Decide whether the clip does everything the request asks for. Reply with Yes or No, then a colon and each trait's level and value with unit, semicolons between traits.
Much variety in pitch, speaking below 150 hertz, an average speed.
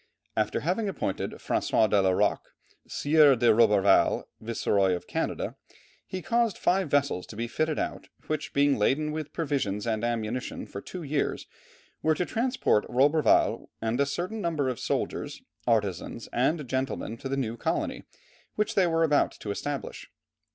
Yes: wide, 5.9 semitones; low, 135 Hz; average, 160 wpm